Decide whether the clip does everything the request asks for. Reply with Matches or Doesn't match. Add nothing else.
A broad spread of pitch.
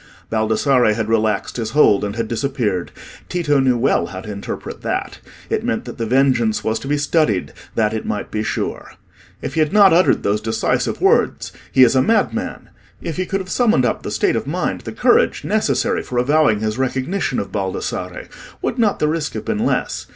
Matches